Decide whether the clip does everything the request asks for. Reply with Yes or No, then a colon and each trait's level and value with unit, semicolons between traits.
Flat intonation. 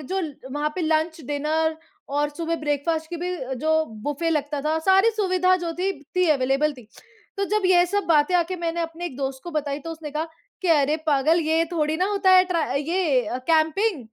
No: average, 3.1 semitones